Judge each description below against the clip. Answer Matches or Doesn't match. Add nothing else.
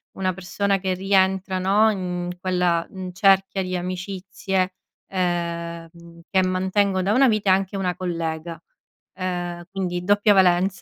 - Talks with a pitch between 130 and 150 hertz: Doesn't match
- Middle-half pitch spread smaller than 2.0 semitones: Matches